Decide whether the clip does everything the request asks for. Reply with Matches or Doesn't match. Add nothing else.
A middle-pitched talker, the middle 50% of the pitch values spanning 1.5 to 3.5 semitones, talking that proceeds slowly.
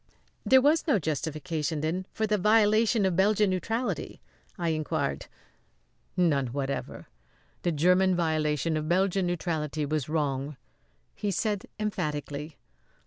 Doesn't match